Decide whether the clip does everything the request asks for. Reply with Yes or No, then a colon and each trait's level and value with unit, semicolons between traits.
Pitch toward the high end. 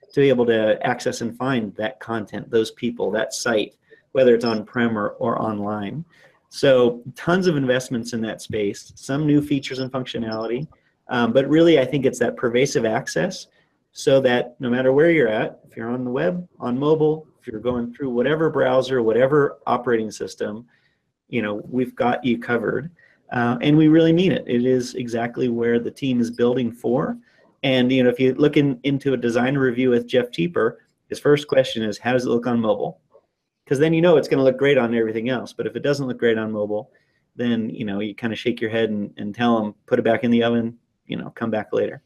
No: low, 125 Hz